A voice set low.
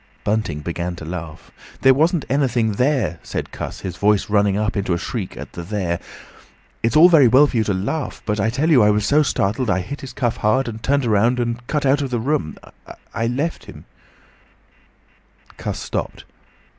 Yes: low, 115 Hz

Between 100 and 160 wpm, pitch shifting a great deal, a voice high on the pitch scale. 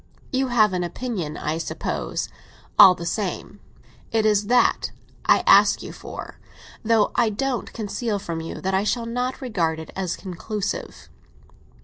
No: average, 150 wpm; average, 4.6 semitones; high, 210 Hz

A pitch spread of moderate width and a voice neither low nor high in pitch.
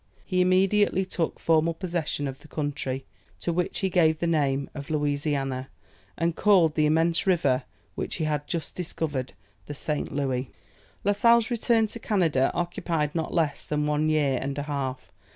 Yes: average, 3.6 semitones; medium, 155 Hz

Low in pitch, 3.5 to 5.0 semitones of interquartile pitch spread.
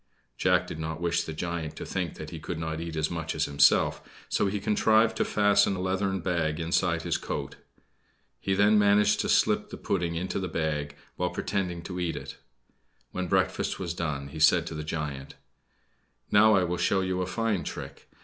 No: very low, 85 Hz; average, 3.0 semitones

